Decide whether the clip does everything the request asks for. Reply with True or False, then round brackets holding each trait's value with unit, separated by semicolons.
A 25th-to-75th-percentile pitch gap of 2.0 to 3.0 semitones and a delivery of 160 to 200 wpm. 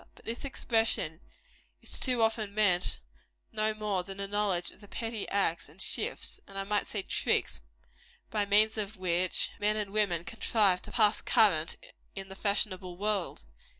True (2.4 semitones; 170 wpm)